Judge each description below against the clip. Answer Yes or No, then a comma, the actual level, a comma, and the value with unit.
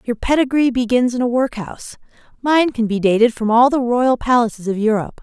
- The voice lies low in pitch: No, high, 240 Hz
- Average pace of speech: Yes, average, 195 wpm